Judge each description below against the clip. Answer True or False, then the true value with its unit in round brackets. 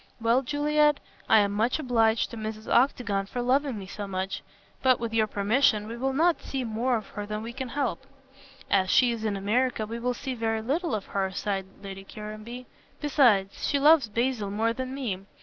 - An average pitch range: True (3.8 semitones)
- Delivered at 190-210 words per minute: True (200 wpm)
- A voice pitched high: True (230 Hz)